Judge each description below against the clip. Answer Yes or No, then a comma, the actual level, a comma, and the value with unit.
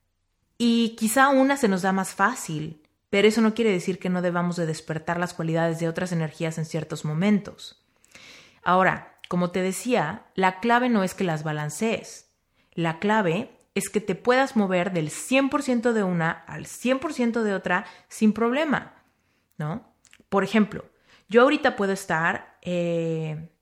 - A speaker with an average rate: Yes, average, 160 wpm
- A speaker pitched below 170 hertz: No, high, 190 Hz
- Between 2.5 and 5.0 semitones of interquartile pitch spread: No, wide, 5.6 semitones